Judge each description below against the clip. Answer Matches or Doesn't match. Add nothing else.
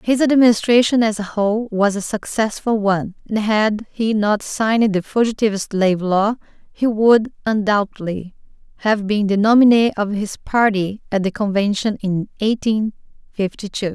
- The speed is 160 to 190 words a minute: Doesn't match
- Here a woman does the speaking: Matches